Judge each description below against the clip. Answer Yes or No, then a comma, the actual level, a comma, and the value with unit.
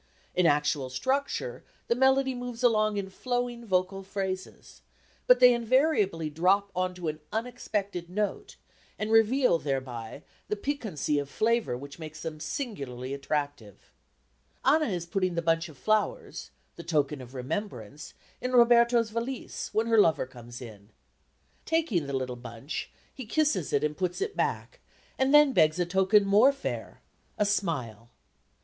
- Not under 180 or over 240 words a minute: No, average, 150 wpm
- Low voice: No, high, 190 Hz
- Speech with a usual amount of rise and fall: No, wide, 8.2 semitones